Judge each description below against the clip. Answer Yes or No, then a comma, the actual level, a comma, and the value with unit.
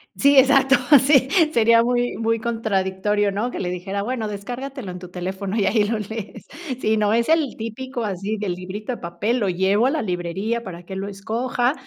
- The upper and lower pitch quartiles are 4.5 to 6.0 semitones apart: No, average, 4.0 semitones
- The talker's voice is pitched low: No, high, 215 Hz